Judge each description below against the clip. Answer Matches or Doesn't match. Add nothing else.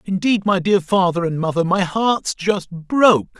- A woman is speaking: Doesn't match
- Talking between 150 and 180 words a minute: Matches